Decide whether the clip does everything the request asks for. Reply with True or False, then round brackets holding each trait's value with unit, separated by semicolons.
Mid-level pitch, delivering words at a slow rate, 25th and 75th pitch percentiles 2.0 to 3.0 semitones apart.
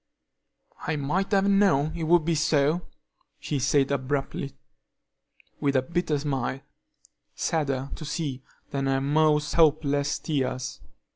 True (145 Hz; 125 wpm; 2.7 semitones)